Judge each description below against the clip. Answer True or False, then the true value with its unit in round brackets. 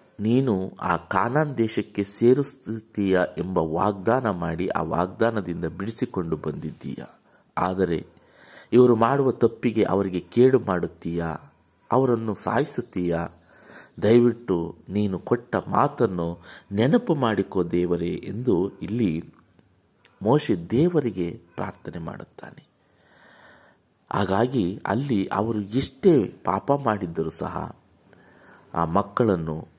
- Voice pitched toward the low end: True (105 Hz)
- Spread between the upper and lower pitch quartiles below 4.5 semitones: False (5.1 semitones)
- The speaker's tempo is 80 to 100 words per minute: True (85 wpm)